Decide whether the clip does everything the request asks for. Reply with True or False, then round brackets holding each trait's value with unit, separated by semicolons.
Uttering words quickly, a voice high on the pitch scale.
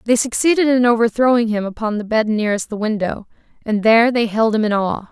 True (210 wpm; 225 Hz)